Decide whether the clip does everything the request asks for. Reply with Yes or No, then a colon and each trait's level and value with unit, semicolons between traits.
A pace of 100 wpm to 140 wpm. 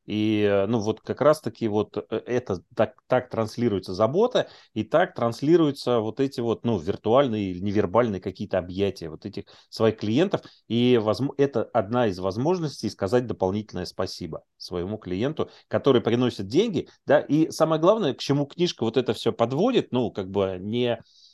No: average, 155 wpm